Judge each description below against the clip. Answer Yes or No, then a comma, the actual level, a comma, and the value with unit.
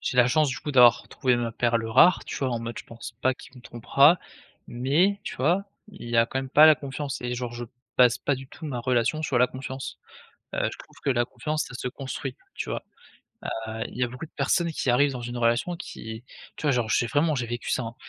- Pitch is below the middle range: Yes, low, 125 Hz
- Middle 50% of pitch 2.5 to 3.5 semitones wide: Yes, average, 3.2 semitones